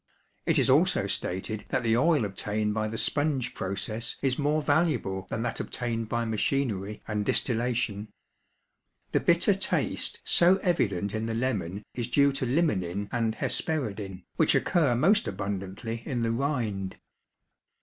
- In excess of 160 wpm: No, average, 145 wpm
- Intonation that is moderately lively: Yes, average, 4.7 semitones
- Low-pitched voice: Yes, low, 115 Hz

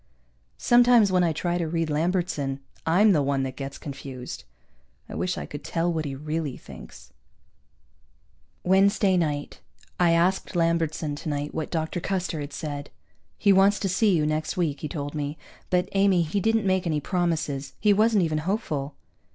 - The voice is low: No, medium, 165 Hz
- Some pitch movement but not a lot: Yes, average, 4.2 semitones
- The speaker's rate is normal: Yes, average, 170 wpm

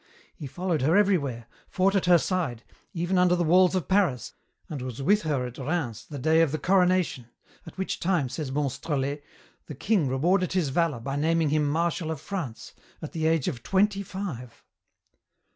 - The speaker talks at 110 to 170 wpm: No, average, 180 wpm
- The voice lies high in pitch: No, medium, 160 Hz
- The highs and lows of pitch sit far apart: No, average, 5.0 semitones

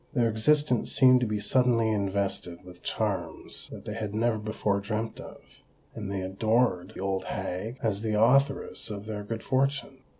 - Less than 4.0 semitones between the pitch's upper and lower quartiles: Yes, average, 3.2 semitones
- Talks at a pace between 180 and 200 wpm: No, average, 170 wpm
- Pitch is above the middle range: No, low, 110 Hz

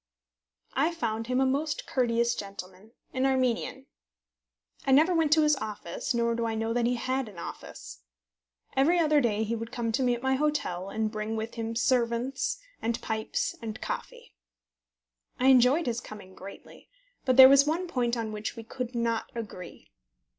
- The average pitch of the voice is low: No, high, 235 Hz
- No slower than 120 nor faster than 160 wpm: No, average, 175 wpm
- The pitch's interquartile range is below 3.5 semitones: Yes, average, 3.1 semitones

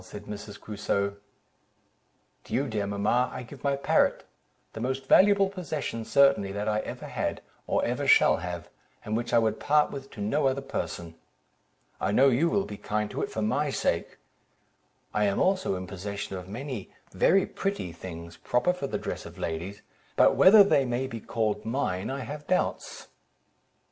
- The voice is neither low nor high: No, low, 115 Hz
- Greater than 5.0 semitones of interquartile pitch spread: Yes, wide, 5.6 semitones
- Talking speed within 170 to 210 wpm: Yes, average, 180 wpm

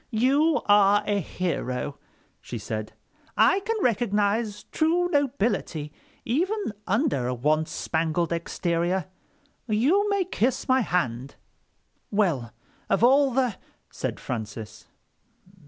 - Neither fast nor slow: No, slow, 105 wpm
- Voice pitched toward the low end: No, high, 205 Hz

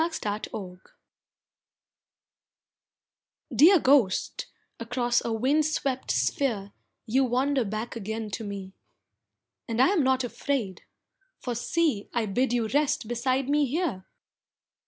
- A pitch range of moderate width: Yes, average, 4.3 semitones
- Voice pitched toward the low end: No, high, 245 Hz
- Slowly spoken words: Yes, slow, 115 wpm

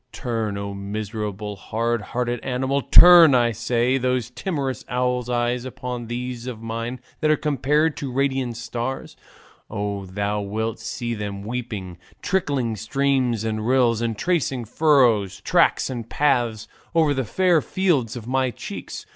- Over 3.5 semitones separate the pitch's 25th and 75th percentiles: No, average, 3.2 semitones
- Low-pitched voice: Yes, low, 120 Hz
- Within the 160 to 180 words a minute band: No, average, 145 wpm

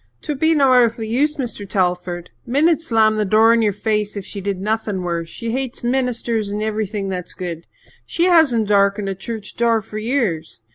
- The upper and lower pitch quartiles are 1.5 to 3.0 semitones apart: No, average, 3.5 semitones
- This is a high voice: Yes, high, 220 Hz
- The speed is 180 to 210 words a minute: Yes, average, 190 wpm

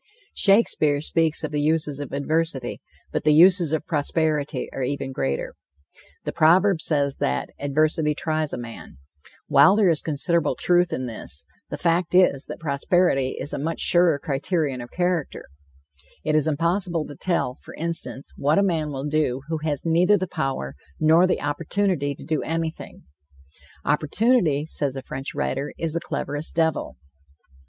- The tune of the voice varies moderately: Yes, average, 3.0 semitones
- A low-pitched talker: No, medium, 155 Hz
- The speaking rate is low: No, average, 160 wpm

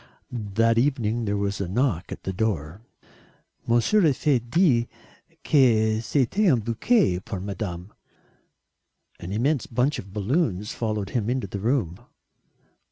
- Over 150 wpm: No, slow, 135 wpm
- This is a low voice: Yes, low, 115 Hz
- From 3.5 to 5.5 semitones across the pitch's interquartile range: Yes, average, 4.4 semitones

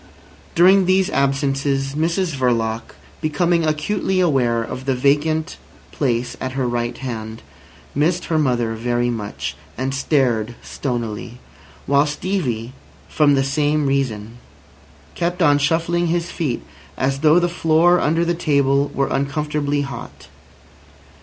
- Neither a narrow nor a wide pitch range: Yes, average, 4.5 semitones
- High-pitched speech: No, medium, 140 Hz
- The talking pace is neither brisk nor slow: No, slow, 125 wpm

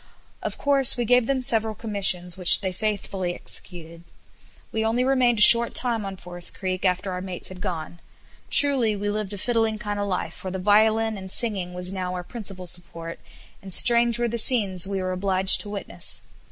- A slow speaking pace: No, average, 195 wpm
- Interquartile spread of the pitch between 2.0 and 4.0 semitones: Yes, average, 3.6 semitones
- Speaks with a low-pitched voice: No, high, 200 Hz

